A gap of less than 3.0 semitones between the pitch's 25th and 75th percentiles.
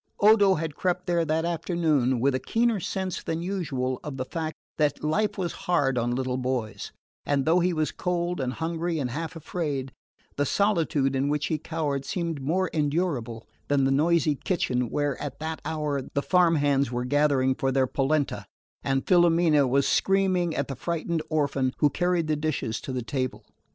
No: average, 4.1 semitones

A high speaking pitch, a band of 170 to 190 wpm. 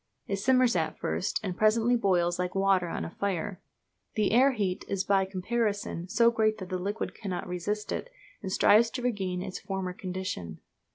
Yes: high, 195 Hz; average, 180 wpm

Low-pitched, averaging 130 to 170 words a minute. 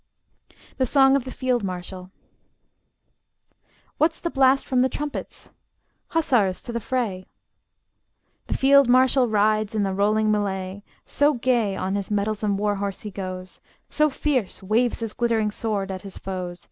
No: high, 215 Hz; average, 150 wpm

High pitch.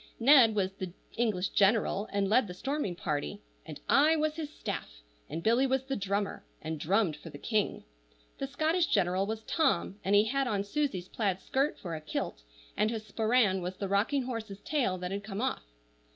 Yes: high, 210 Hz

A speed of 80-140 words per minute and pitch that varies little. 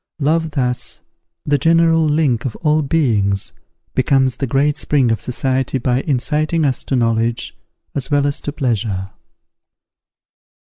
No: slow, 135 wpm; average, 3.8 semitones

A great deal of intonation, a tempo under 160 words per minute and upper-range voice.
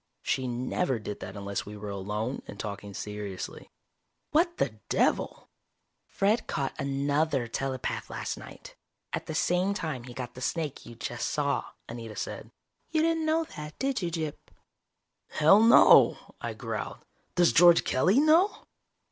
No: wide, 7.7 semitones; average, 150 wpm; medium, 140 Hz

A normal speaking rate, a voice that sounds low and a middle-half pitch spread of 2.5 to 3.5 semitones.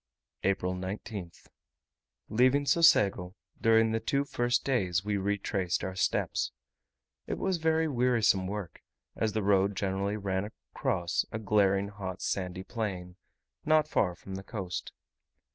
No: slow, 130 wpm; low, 100 Hz; average, 3.2 semitones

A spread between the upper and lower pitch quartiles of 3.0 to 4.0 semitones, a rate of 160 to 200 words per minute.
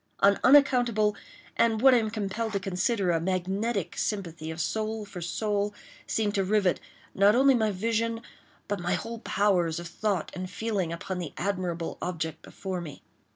Yes: average, 3.5 semitones; average, 165 wpm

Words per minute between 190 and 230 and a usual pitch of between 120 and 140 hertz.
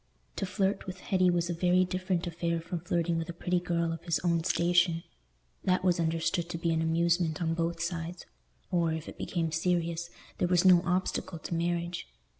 No: average, 195 wpm; medium, 170 Hz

